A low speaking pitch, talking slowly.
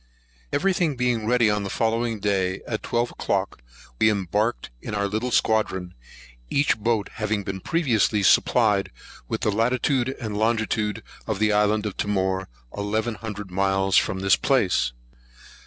No: low, 105 Hz; average, 150 wpm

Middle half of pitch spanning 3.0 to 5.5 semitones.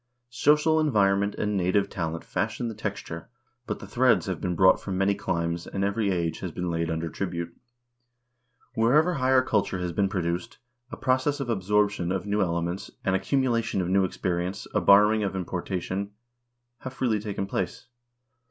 Yes: average, 3.9 semitones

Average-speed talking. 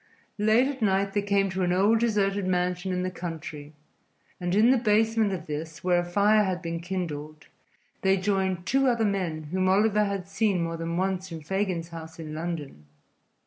Yes: average, 185 wpm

